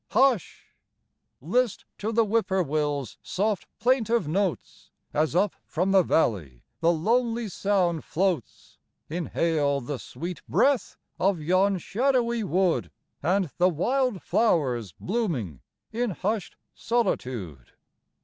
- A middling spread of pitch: No, wide, 6.4 semitones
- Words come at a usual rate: No, slow, 115 wpm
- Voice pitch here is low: No, medium, 185 Hz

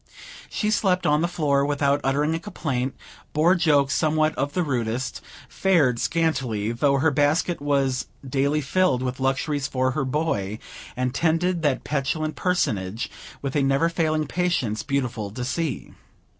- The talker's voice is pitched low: No, medium, 145 Hz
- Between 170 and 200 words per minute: No, average, 150 wpm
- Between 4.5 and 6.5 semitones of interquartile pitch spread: No, average, 3.7 semitones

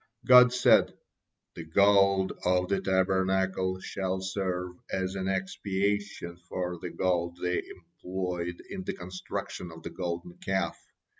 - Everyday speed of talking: No, slow, 130 wpm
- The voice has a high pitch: No, very low, 95 Hz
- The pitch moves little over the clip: Yes, narrow, 1.4 semitones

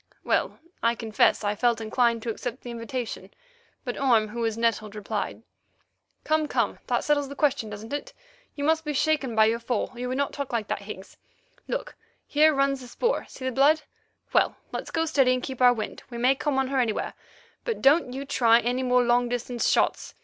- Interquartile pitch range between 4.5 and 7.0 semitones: No, average, 3.2 semitones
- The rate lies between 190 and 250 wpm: Yes, fast, 205 wpm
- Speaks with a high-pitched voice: Yes, very high, 250 Hz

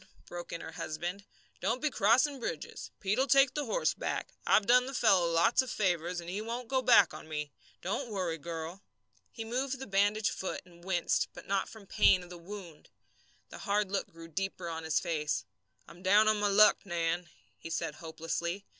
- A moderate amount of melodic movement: Yes, average, 4.6 semitones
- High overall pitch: Yes, high, 195 Hz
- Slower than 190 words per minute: No, average, 200 wpm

